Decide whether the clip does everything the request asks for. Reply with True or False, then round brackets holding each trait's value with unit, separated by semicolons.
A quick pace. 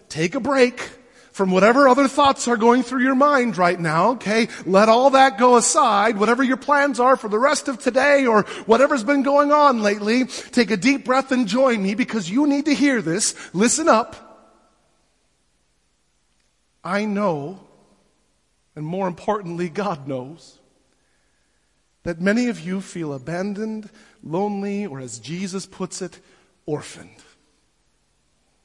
False (145 wpm)